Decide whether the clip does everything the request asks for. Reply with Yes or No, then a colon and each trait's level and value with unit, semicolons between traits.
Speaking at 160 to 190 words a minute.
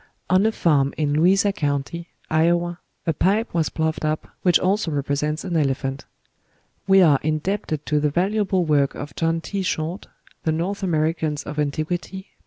Yes: average, 165 wpm